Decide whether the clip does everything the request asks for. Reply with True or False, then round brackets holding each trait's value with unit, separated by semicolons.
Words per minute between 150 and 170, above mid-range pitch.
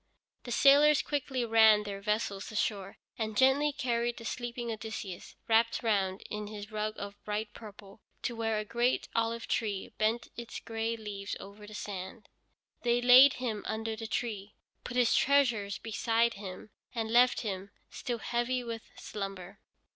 True (155 wpm; 225 Hz)